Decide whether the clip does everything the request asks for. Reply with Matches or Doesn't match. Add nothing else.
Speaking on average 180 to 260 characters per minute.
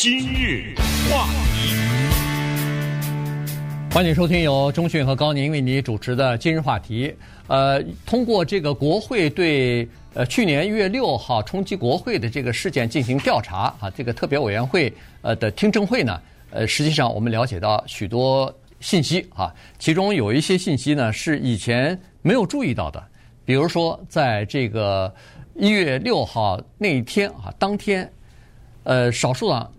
Matches